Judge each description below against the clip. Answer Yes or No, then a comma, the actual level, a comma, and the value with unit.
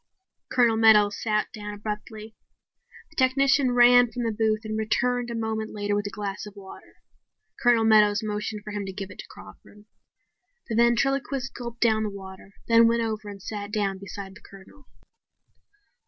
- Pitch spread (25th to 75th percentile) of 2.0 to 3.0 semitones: Yes, narrow, 2.4 semitones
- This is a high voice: Yes, high, 215 Hz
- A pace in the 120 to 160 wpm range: No, average, 170 wpm